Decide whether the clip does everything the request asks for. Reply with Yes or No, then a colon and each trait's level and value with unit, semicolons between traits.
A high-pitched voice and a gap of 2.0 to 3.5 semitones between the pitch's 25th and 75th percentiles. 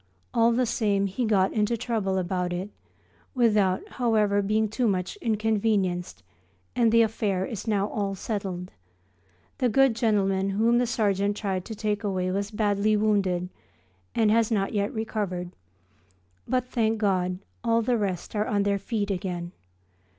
Yes: high, 205 Hz; narrow, 2.6 semitones